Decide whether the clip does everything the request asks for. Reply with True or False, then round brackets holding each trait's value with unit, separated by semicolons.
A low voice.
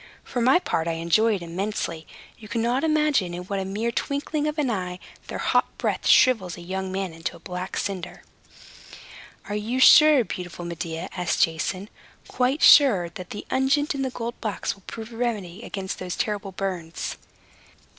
False (200 Hz)